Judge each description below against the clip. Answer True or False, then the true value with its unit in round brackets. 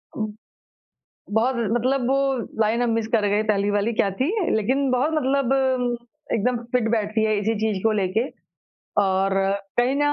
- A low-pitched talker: False (225 Hz)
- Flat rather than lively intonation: False (3.5 semitones)